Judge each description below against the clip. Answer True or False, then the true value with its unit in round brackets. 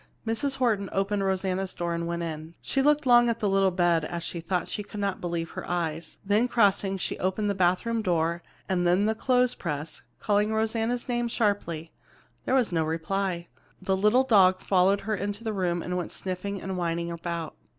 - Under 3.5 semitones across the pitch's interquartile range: False (4.0 semitones)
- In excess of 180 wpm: True (190 wpm)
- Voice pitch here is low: False (190 Hz)